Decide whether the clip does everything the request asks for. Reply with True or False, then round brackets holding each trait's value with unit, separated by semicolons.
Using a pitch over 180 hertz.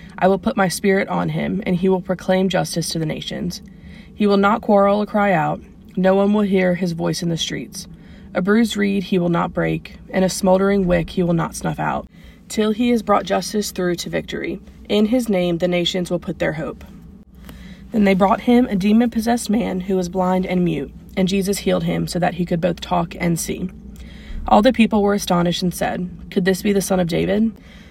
True (190 Hz)